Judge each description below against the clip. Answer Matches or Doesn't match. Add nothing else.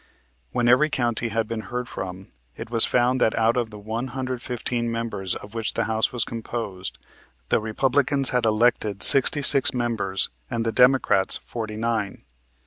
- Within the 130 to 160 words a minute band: Doesn't match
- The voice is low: Matches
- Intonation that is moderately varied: Doesn't match